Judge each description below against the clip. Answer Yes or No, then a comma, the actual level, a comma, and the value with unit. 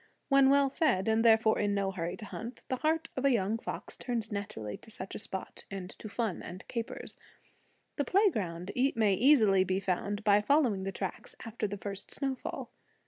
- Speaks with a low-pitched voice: No, high, 215 Hz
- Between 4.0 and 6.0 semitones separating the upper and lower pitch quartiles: Yes, average, 4.6 semitones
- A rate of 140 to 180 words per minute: No, average, 190 wpm